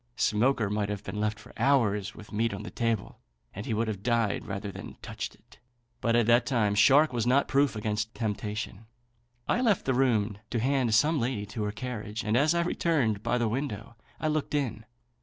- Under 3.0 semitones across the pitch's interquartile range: No, average, 3.8 semitones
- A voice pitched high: No, low, 115 Hz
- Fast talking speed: Yes, fast, 210 wpm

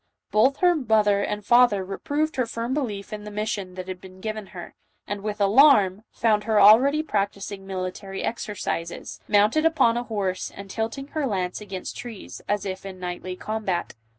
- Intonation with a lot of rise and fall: No, average, 3.2 semitones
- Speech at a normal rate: Yes, average, 175 wpm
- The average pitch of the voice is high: Yes, high, 210 Hz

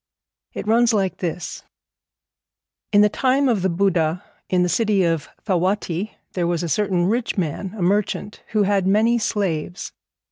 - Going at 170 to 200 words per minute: No, average, 155 wpm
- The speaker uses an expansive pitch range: No, average, 3.2 semitones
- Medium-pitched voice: No, high, 195 Hz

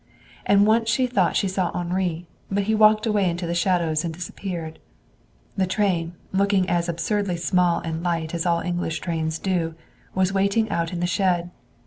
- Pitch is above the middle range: No, medium, 180 Hz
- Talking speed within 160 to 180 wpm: Yes, average, 175 wpm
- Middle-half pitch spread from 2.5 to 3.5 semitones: Yes, average, 2.8 semitones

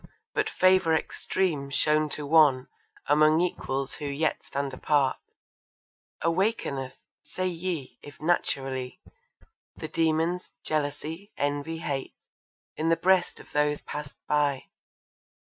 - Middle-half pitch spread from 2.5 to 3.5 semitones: Yes, average, 2.8 semitones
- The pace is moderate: No, slow, 110 wpm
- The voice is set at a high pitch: No, medium, 150 Hz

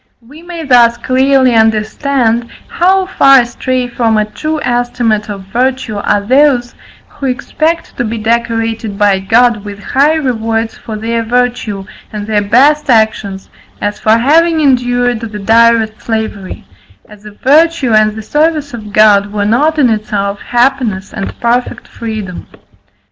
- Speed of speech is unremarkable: Yes, average, 145 wpm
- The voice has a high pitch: Yes, high, 235 Hz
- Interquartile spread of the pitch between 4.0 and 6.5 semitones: No, average, 3.5 semitones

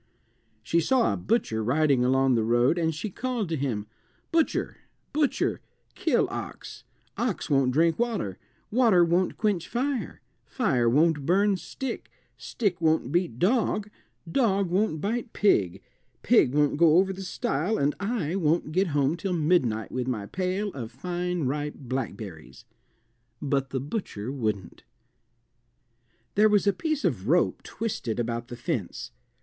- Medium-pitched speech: Yes, medium, 165 Hz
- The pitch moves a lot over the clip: Yes, wide, 7.6 semitones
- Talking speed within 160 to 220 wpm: No, average, 145 wpm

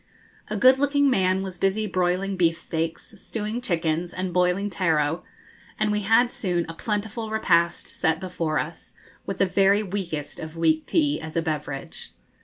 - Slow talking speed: No, average, 165 wpm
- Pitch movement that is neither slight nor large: Yes, average, 4.1 semitones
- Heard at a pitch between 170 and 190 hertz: Yes, medium, 185 Hz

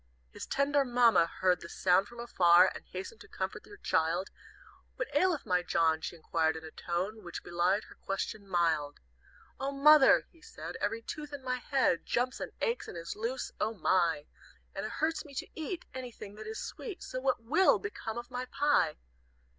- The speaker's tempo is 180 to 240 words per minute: Yes, average, 190 wpm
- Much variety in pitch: Yes, wide, 7.9 semitones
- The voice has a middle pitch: No, high, 225 Hz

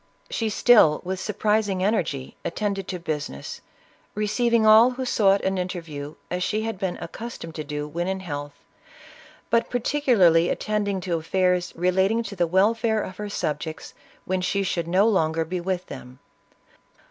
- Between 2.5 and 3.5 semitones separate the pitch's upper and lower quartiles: No, average, 4.2 semitones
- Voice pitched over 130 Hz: Yes, high, 190 Hz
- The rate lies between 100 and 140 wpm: No, average, 160 wpm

